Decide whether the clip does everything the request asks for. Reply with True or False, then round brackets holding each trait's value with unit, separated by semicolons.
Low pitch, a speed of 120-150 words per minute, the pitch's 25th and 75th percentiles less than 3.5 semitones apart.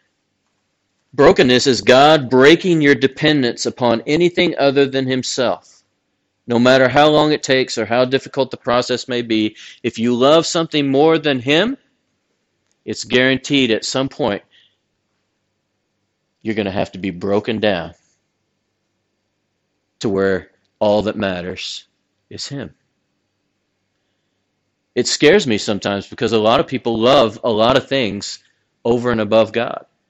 False (120 Hz; 140 wpm; 4.4 semitones)